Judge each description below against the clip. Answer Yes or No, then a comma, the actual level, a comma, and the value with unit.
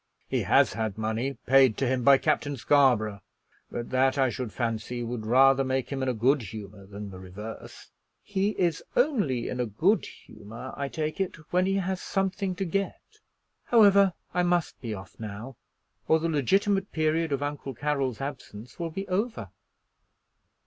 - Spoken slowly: No, average, 170 wpm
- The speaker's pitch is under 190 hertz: Yes, low, 135 Hz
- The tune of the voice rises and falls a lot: Yes, wide, 7.3 semitones